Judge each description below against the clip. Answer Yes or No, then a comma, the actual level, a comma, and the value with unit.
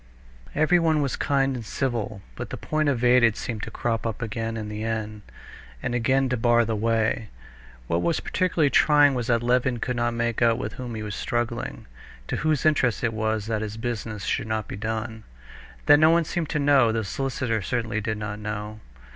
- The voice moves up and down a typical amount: Yes, average, 3.3 semitones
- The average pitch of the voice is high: No, low, 115 Hz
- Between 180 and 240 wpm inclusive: Yes, average, 195 wpm